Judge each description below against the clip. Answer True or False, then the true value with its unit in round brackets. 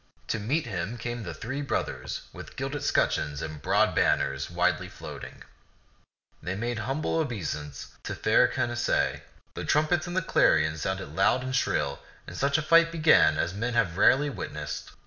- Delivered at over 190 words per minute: False (165 wpm)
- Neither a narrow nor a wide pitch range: False (8.5 semitones)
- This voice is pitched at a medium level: False (115 Hz)